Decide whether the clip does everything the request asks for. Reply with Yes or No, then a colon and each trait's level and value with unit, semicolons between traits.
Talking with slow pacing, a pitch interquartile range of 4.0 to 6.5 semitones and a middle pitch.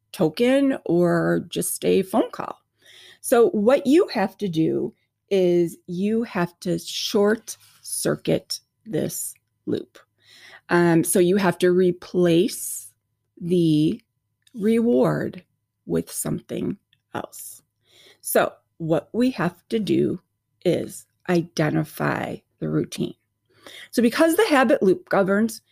Yes: slow, 110 wpm; average, 4.9 semitones; medium, 175 Hz